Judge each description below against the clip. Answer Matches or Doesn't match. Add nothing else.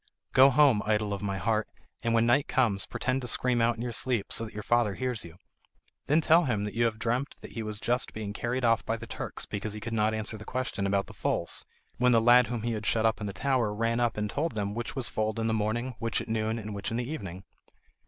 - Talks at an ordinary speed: Doesn't match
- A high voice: Doesn't match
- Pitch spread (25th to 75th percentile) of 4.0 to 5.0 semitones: Doesn't match